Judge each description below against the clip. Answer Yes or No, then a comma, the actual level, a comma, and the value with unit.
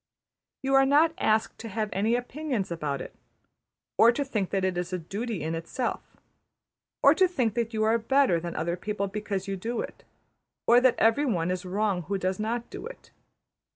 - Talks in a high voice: Yes, high, 215 Hz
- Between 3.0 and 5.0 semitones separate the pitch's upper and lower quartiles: Yes, average, 4.7 semitones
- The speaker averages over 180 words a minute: Yes, average, 195 wpm